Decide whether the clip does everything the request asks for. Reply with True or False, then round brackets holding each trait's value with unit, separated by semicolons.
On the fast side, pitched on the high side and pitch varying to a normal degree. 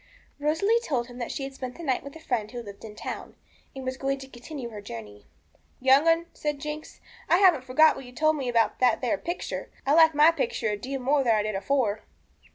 True (240 wpm; 265 Hz; 4.4 semitones)